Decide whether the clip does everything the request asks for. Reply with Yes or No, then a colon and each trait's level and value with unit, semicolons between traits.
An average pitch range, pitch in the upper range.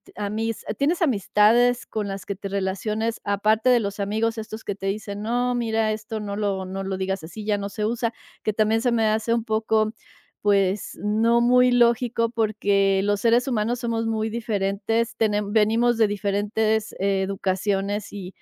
No: narrow, 2.2 semitones; high, 215 Hz